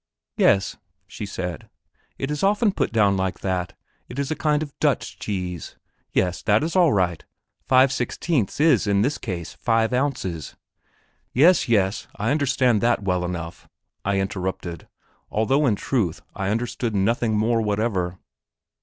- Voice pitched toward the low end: Yes, low, 110 Hz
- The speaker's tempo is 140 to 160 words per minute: Yes, average, 150 wpm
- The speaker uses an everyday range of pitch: No, wide, 5.9 semitones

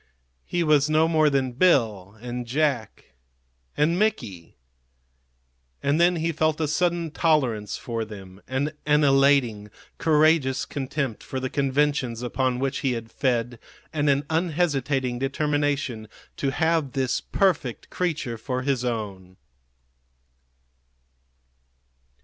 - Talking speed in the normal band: No, slow, 120 wpm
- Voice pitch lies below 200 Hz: Yes, low, 135 Hz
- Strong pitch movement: No, average, 4.1 semitones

